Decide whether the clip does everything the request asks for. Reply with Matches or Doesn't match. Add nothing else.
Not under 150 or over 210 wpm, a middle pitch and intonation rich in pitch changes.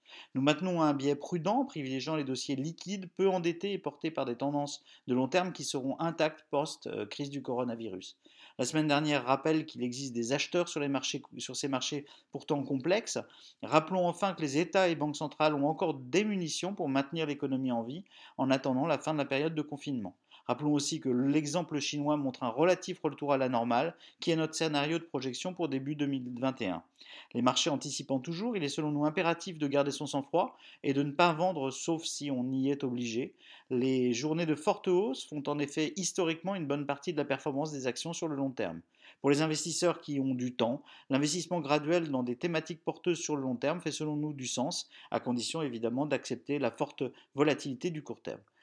Doesn't match